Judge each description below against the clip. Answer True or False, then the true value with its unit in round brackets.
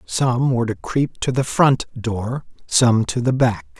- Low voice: True (125 Hz)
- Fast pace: False (190 wpm)